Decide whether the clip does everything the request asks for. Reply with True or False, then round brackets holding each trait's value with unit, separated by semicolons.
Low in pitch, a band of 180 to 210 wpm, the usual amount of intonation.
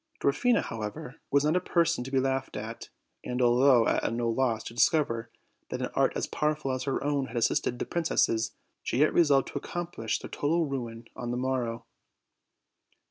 True (130 Hz; 190 wpm; 3.9 semitones)